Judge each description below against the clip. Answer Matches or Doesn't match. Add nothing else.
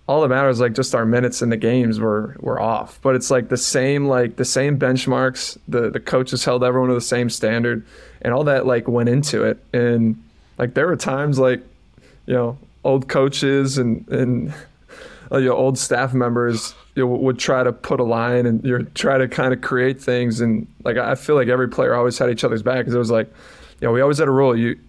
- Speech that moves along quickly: Matches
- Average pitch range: Doesn't match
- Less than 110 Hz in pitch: Doesn't match